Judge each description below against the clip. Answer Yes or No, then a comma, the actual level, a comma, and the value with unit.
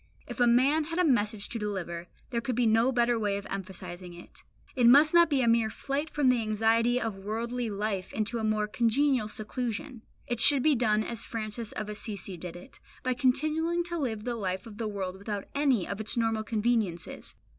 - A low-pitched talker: No, high, 225 Hz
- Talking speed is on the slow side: No, fast, 205 wpm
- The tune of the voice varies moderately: Yes, average, 3.3 semitones